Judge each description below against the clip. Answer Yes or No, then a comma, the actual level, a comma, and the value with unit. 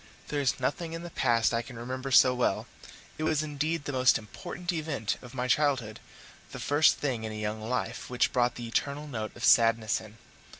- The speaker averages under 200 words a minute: No, fast, 205 wpm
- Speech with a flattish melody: No, average, 4.1 semitones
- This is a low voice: Yes, low, 125 Hz